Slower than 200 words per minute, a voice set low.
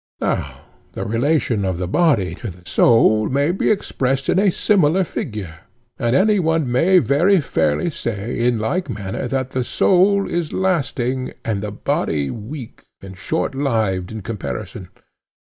Yes: average, 150 wpm; low, 125 Hz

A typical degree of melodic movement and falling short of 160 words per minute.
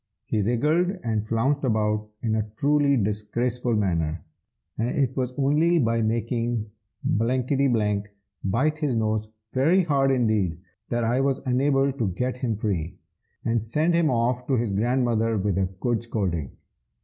Yes: average, 3.9 semitones; average, 150 wpm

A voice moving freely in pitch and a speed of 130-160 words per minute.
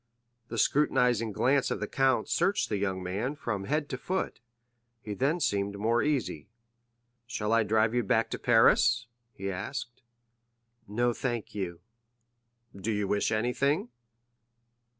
No: average, 4.4 semitones; average, 140 wpm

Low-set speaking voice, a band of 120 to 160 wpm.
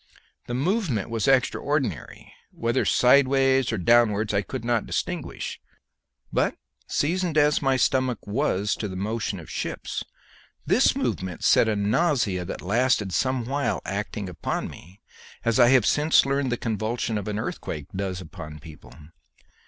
Yes: low, 115 Hz; average, 150 wpm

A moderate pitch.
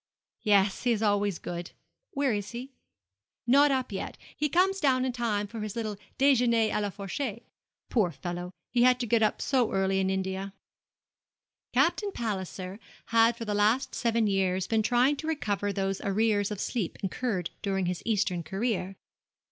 No: high, 215 Hz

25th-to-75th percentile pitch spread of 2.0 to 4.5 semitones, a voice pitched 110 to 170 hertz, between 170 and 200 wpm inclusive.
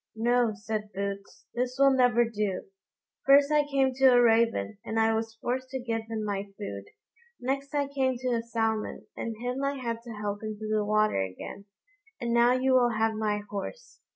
No: average, 3.2 semitones; high, 230 Hz; average, 190 wpm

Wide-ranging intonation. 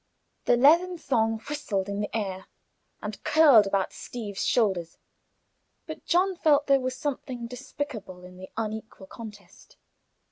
Yes: wide, 6.2 semitones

